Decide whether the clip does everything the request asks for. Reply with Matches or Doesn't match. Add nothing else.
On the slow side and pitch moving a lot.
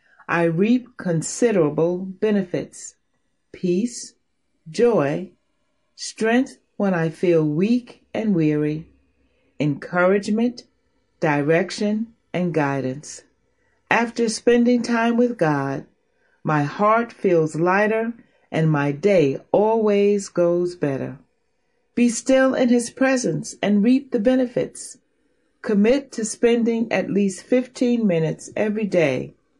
Matches